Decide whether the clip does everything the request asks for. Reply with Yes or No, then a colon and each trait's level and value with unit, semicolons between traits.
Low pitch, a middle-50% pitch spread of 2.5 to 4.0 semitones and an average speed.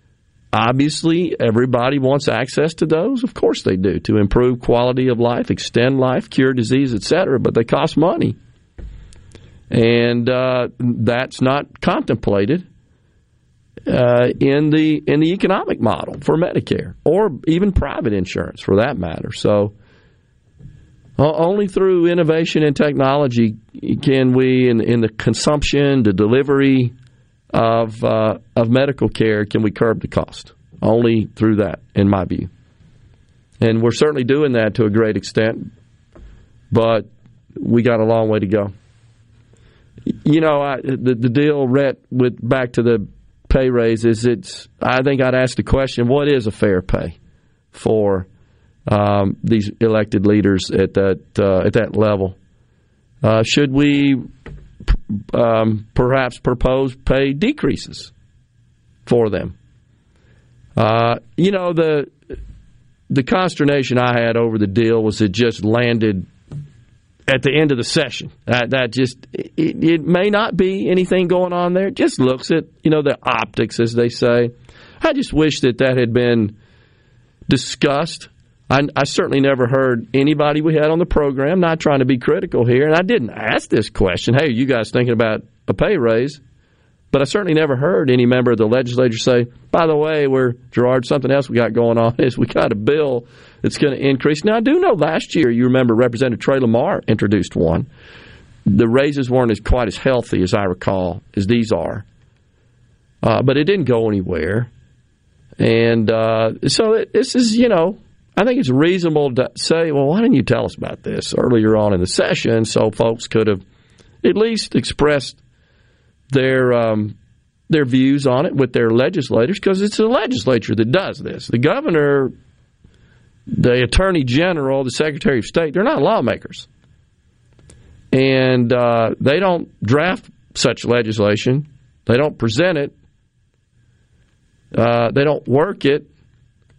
Yes: low, 125 Hz; average, 3.7 semitones; average, 160 wpm